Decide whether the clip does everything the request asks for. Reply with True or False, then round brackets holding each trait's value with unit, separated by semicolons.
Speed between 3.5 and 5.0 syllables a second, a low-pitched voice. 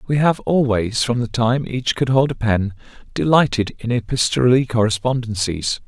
True (4.9 syllables/s; 120 Hz)